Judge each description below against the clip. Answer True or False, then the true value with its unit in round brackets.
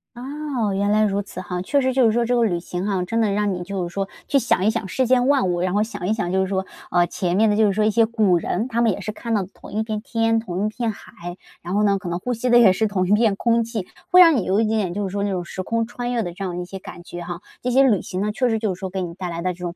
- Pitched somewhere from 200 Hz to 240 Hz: True (205 Hz)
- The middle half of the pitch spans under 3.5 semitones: False (3.9 semitones)